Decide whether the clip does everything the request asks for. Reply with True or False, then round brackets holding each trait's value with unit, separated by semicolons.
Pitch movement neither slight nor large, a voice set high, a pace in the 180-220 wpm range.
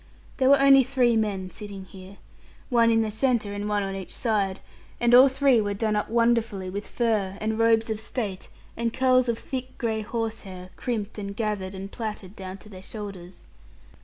True (3.0 semitones; 215 Hz; 190 wpm)